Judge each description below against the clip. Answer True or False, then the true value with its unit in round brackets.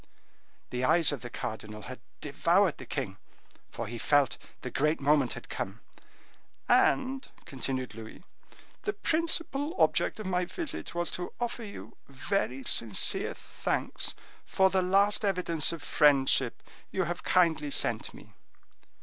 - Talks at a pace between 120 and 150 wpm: True (140 wpm)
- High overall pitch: False (160 Hz)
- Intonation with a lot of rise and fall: True (7.0 semitones)